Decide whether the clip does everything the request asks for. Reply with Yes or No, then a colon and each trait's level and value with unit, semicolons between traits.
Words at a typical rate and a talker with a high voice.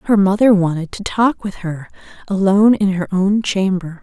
Yes: average, 180 wpm; high, 195 Hz